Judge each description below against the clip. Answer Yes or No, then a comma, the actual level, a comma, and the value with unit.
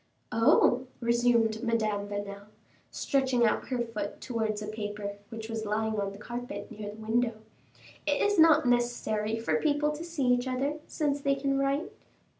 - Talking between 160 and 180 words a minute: Yes, average, 165 wpm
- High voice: Yes, high, 235 Hz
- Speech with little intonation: No, average, 4.0 semitones